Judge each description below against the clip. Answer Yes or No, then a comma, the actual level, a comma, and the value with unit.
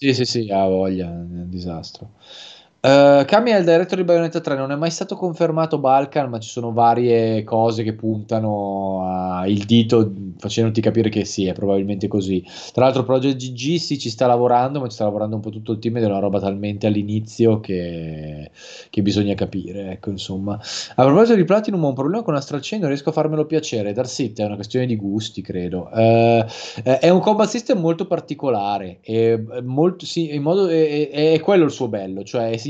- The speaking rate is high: Yes, fast, 200 wpm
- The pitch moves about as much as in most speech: No, wide, 6.3 semitones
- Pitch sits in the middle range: No, low, 115 Hz